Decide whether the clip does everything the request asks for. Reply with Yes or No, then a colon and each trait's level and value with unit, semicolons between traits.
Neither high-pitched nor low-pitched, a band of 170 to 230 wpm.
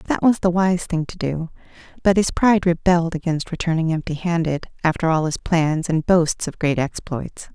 Yes: medium, 170 Hz; average, 190 wpm